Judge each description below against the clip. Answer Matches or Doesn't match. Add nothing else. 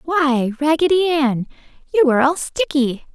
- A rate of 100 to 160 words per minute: Matches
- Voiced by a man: Doesn't match